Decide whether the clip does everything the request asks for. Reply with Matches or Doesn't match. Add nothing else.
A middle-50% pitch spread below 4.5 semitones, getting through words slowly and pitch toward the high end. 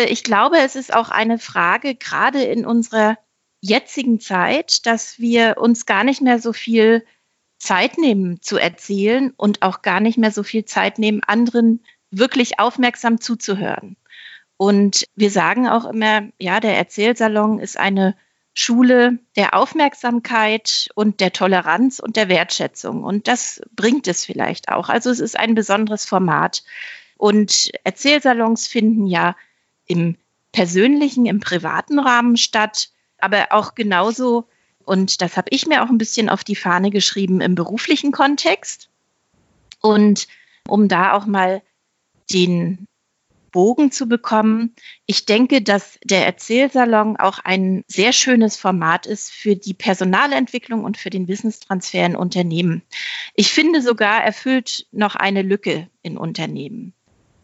Doesn't match